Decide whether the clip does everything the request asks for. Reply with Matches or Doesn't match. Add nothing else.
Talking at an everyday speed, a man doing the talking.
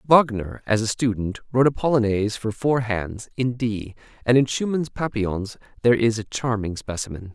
Matches